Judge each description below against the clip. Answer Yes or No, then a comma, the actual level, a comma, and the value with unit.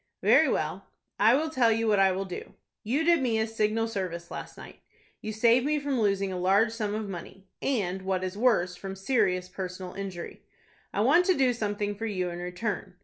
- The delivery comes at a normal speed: No, fast, 210 wpm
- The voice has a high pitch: Yes, high, 205 Hz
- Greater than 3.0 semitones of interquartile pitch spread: Yes, average, 3.5 semitones